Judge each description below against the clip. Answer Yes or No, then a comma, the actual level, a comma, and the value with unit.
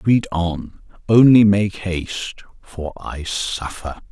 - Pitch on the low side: Yes, very low, 95 Hz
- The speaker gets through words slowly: Yes, slow, 115 wpm